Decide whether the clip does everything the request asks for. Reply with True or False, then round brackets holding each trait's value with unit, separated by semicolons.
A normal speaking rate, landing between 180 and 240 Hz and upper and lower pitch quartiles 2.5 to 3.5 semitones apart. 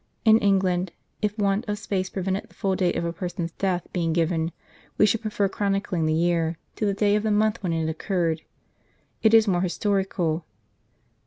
True (185 wpm; 190 Hz; 3.2 semitones)